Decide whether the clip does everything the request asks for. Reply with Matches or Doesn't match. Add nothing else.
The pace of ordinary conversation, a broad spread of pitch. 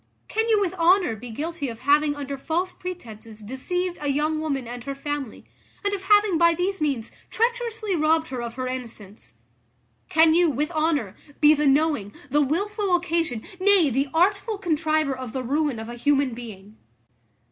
Matches